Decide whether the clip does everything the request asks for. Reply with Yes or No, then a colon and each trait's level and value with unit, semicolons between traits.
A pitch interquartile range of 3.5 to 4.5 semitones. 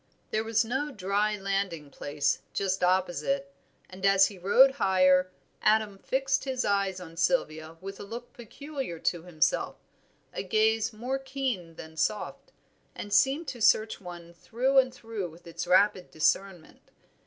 No: average, 5.2 semitones